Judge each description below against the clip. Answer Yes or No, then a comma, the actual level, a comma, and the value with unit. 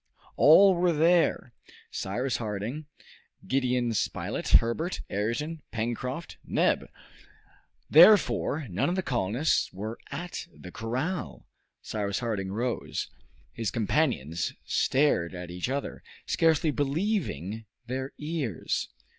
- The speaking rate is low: Yes, slow, 105 wpm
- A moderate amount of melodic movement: No, wide, 6.8 semitones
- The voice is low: Yes, low, 125 Hz